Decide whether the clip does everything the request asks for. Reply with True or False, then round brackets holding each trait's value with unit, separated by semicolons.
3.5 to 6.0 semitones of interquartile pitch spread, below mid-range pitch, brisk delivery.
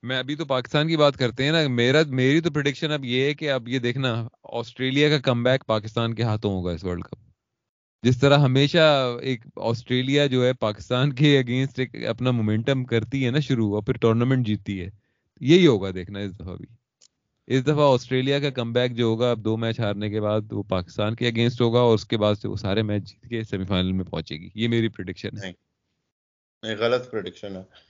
True (3.9 semitones; 120 Hz; 215 wpm)